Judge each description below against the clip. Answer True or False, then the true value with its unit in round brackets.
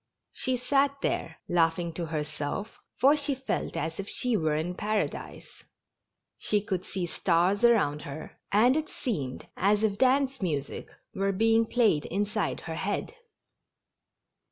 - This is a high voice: True (200 Hz)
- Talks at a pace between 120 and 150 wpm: True (140 wpm)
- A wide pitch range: True (6.3 semitones)